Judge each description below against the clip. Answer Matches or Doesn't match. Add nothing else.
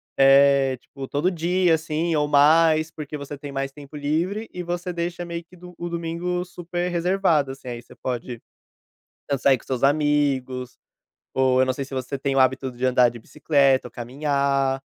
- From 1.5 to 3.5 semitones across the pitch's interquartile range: Doesn't match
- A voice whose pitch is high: Doesn't match